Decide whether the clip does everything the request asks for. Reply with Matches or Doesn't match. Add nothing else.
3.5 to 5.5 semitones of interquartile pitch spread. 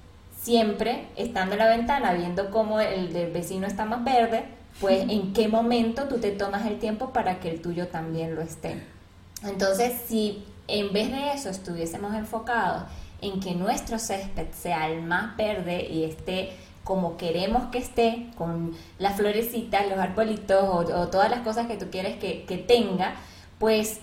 Matches